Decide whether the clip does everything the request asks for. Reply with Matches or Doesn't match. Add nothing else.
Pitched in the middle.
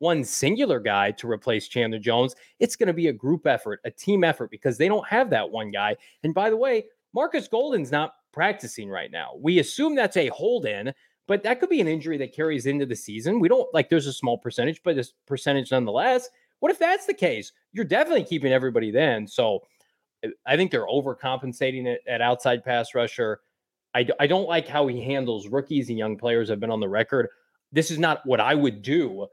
Matches